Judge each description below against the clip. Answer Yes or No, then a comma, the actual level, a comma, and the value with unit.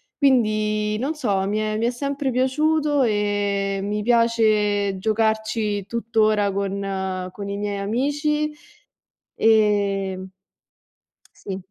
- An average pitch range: Yes, average, 3.0 semitones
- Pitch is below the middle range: No, high, 215 Hz